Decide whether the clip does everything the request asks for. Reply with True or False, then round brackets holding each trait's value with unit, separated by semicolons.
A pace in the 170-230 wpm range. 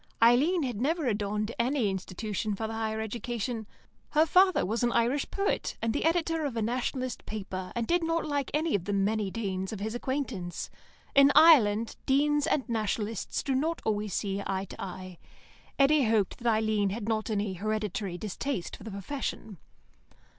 True (175 wpm)